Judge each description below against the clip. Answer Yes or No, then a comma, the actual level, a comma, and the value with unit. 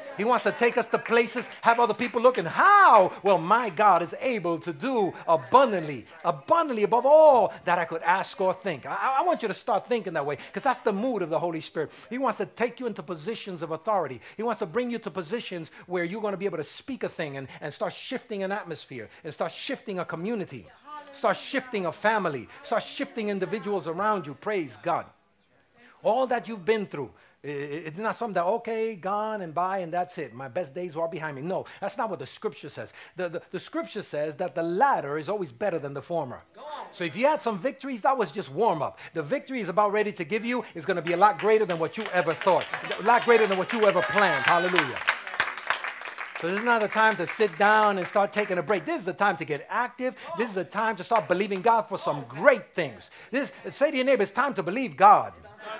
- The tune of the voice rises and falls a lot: No, average, 5.0 semitones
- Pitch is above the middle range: Yes, high, 210 Hz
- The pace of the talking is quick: Yes, fast, 240 wpm